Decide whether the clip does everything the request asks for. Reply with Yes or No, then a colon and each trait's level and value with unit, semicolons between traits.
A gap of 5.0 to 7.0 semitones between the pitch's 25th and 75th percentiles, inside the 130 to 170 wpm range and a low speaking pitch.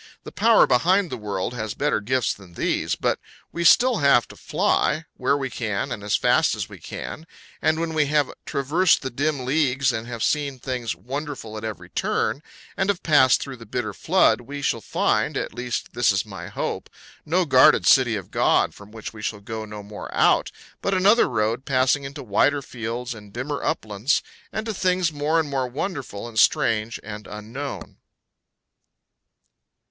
No: average, 5.3 semitones; average, 185 wpm; low, 130 Hz